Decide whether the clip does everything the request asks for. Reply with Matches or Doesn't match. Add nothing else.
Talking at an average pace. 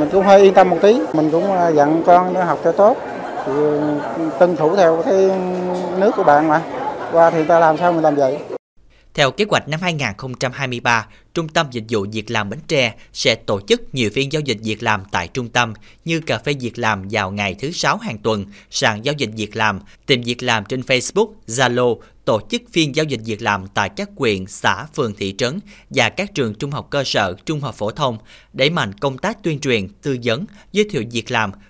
Matches